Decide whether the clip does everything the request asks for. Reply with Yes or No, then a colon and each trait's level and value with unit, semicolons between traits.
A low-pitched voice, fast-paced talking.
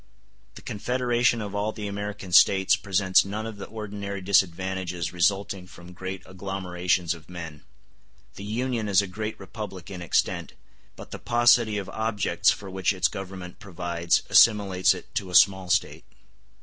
No: very low, 95 Hz; average, 155 wpm